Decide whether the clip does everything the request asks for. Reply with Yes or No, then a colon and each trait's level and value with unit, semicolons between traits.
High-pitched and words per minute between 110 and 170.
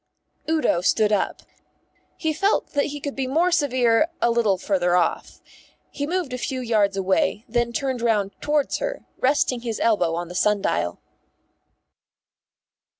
Yes: high, 235 Hz; average, 150 wpm